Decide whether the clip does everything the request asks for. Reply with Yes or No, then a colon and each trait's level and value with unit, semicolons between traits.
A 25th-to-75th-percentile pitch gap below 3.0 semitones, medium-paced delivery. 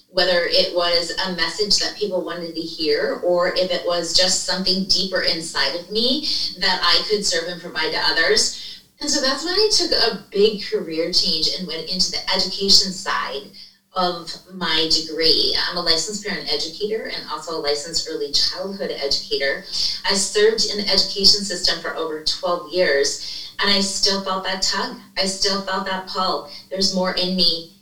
Yes: narrow, 2.5 semitones; average, 180 wpm